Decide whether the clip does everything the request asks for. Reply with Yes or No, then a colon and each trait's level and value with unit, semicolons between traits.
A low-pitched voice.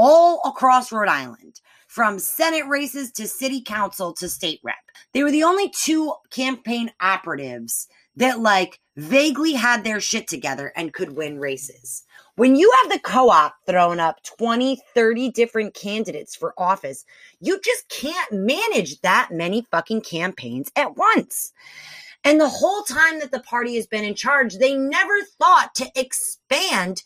No: high, 240 Hz